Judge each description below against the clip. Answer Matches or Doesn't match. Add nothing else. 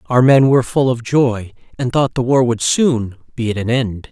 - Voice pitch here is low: Matches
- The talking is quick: Matches